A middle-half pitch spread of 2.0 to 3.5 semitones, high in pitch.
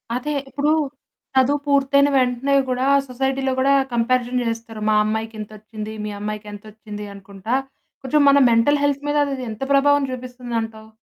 No: average, 4.0 semitones; very high, 250 Hz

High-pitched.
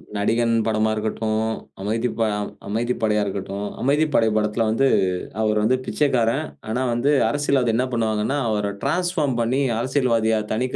No: low, 115 Hz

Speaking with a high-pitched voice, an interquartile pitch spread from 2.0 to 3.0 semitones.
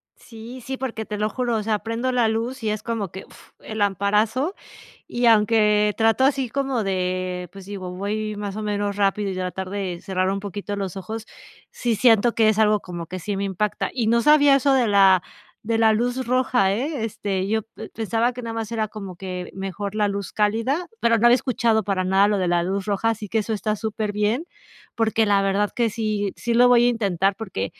Yes: high, 215 Hz; average, 2.7 semitones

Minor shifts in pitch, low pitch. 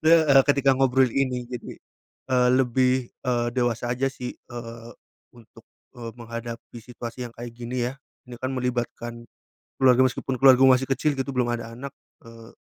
Yes: narrow, 1.9 semitones; low, 125 Hz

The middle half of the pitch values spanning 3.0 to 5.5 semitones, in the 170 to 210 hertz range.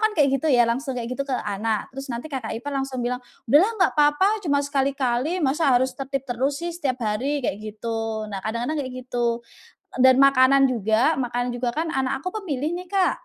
No: average, 3.5 semitones; very high, 265 Hz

